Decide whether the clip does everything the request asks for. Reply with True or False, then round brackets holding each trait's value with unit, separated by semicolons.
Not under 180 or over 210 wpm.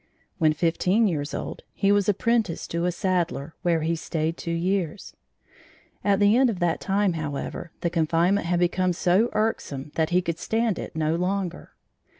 False (170 wpm)